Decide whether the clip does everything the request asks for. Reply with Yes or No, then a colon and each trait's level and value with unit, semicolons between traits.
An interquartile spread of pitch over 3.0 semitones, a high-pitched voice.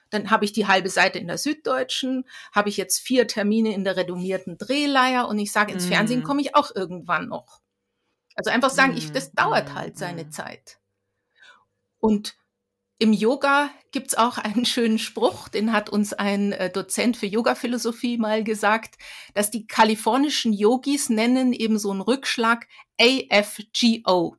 Yes: average, 3.4 semitones; high, 220 Hz